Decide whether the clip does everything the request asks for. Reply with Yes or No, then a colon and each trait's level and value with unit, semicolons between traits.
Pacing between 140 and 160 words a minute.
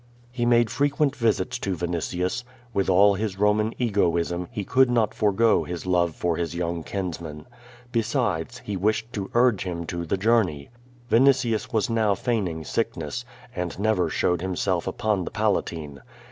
Yes: average, 155 wpm